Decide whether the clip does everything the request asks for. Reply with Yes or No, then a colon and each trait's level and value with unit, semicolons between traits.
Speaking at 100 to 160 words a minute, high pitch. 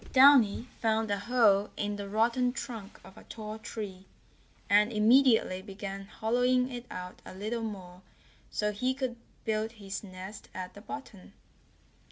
Yes: average, 150 wpm; high, 215 Hz